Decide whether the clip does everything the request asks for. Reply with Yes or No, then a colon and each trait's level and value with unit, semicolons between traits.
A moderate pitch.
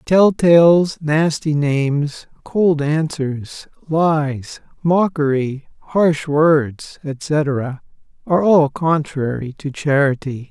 Yes: medium, 150 Hz